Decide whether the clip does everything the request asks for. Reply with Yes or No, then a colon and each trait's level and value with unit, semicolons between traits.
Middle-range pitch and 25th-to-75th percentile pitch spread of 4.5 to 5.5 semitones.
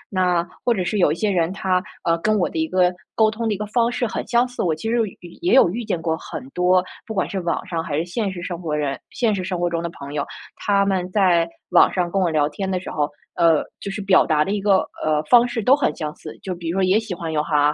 No: medium, 180 Hz; average, 3.7 semitones